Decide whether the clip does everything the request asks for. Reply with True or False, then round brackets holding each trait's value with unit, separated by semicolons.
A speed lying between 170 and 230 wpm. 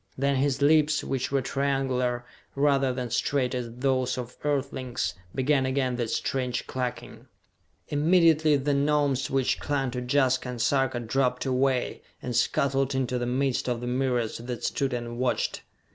False (155 wpm)